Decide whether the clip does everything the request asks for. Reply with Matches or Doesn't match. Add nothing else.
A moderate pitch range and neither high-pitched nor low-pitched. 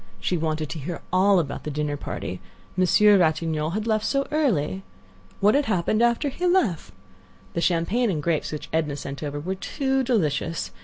Doesn't match